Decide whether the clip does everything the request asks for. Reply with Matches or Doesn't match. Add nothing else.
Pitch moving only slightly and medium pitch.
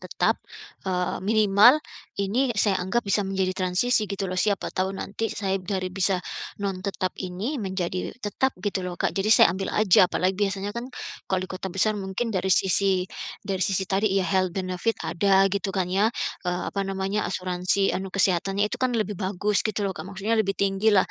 Doesn't match